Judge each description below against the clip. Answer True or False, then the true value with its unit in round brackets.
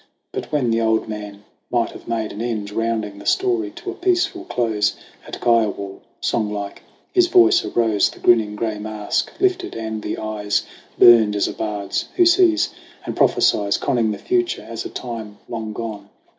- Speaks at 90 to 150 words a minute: False (170 wpm)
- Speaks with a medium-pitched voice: False (115 Hz)